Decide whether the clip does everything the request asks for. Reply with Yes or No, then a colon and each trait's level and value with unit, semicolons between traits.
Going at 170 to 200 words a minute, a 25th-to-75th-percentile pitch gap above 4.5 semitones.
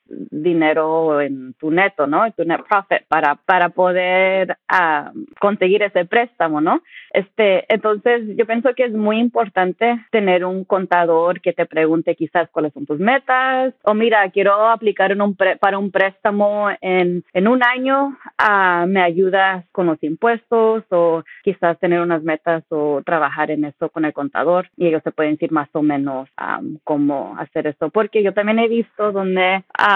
Yes: average, 175 wpm; average, 4.9 semitones